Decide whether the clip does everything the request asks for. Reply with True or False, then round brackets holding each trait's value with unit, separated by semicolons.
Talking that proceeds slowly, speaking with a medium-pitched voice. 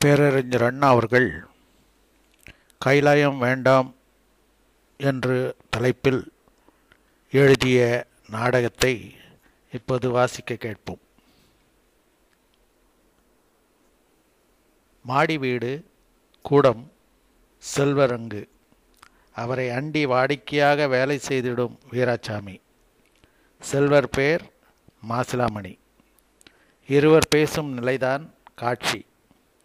False (60 wpm; 130 Hz)